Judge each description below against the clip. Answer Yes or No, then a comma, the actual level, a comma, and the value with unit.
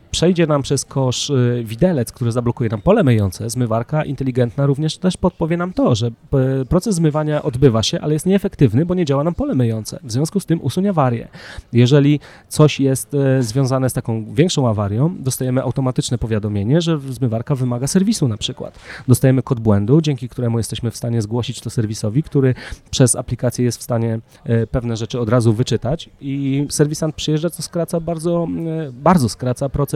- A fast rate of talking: Yes, fast, 170 wpm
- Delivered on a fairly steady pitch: No, average, 4.3 semitones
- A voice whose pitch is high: No, low, 135 Hz